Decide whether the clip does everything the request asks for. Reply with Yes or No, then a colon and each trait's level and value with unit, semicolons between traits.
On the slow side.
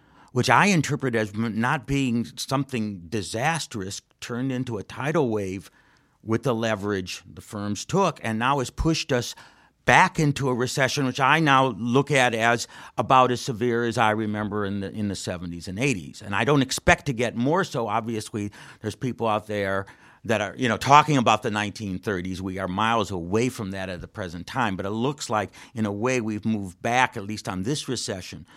No: average, 195 wpm